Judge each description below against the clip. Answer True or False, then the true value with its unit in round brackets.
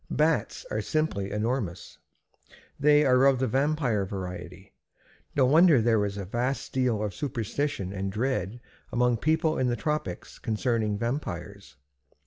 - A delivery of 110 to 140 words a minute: True (135 wpm)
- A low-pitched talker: True (120 Hz)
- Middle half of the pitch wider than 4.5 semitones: True (5.3 semitones)